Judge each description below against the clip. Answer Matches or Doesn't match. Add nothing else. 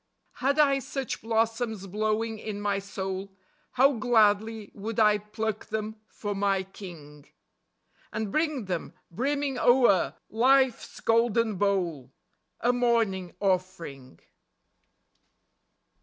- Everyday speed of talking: Doesn't match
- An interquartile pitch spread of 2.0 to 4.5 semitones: Matches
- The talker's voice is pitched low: Doesn't match